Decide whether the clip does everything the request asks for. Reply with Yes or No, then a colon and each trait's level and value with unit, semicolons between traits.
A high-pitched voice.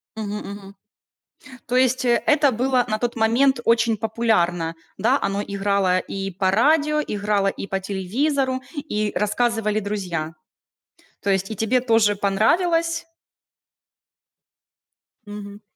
Yes: high, 215 Hz